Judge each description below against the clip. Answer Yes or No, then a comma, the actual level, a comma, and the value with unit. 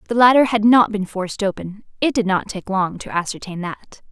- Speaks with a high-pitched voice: Yes, high, 205 Hz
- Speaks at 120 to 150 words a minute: No, fast, 205 wpm